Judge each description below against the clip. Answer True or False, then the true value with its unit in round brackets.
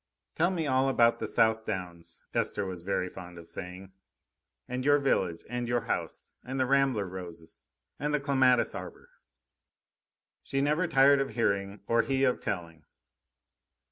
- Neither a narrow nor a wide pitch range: False (6.7 semitones)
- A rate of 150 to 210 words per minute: True (155 wpm)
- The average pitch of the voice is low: True (120 Hz)